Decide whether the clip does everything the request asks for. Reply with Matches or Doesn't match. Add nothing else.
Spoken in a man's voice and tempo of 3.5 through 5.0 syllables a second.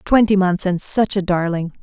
Doesn't match